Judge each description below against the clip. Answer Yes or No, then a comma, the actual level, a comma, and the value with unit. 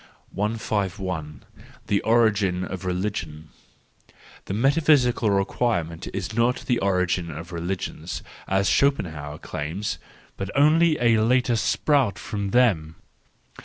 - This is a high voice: No, low, 100 Hz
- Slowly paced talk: Yes, slow, 120 wpm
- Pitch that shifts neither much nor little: Yes, average, 4.9 semitones